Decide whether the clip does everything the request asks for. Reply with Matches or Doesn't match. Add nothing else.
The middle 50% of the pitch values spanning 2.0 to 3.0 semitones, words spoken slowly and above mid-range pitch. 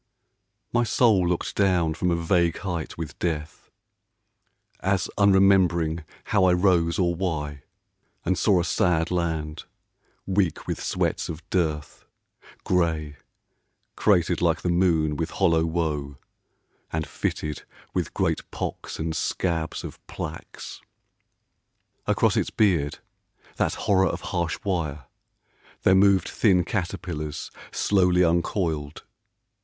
Doesn't match